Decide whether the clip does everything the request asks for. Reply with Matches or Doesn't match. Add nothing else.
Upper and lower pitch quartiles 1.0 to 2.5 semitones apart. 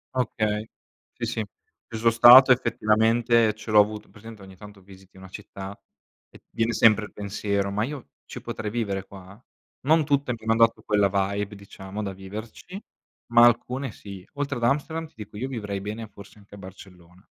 Doesn't match